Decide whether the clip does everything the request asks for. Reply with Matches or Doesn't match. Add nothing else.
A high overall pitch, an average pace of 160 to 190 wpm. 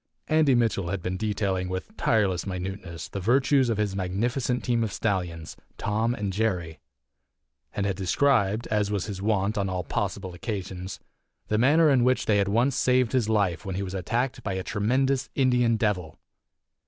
Doesn't match